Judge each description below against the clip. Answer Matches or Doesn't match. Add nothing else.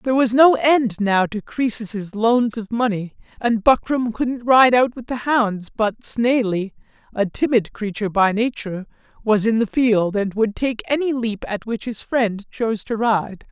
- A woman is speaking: Doesn't match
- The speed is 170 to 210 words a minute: Matches